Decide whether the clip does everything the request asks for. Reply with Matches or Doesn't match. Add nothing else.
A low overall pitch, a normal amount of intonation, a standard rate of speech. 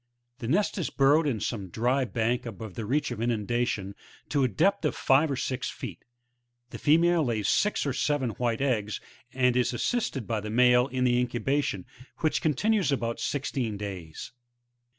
Matches